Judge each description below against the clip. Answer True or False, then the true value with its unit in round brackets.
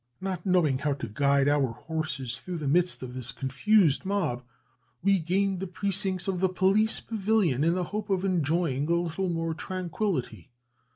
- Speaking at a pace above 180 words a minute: False (170 wpm)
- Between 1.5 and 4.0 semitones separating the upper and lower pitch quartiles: False (5.1 semitones)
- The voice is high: False (175 Hz)